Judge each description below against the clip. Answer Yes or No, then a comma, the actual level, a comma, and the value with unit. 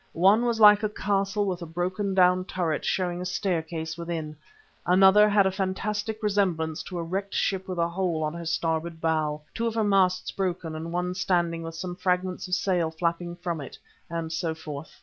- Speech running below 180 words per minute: No, average, 195 wpm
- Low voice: No, medium, 180 Hz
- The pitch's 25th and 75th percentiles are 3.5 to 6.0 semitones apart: No, average, 2.9 semitones